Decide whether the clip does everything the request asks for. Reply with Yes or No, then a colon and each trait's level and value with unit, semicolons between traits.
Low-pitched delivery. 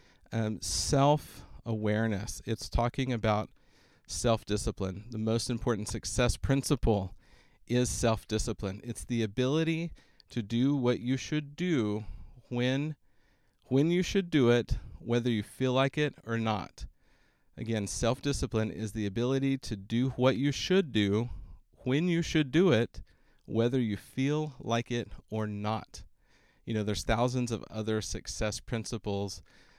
Yes: low, 115 Hz